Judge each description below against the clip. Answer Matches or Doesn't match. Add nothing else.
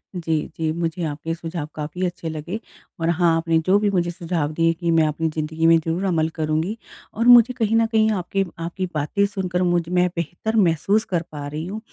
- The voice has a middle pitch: Matches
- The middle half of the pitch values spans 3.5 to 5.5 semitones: Doesn't match